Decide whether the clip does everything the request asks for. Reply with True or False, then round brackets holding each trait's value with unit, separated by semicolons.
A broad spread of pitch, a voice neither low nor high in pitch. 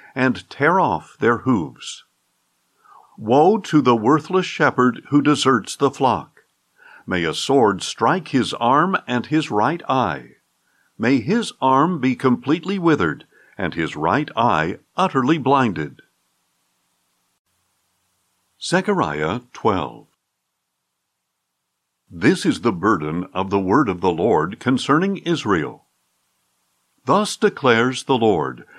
False (8.1 semitones; 130 Hz)